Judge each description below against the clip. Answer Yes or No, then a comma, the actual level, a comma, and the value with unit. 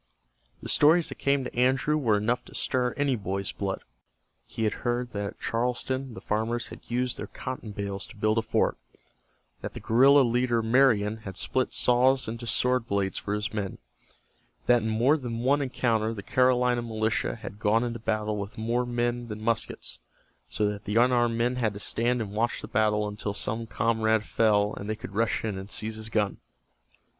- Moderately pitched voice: No, low, 115 Hz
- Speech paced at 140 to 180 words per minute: No, average, 190 wpm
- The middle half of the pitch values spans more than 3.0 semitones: No, narrow, 2.6 semitones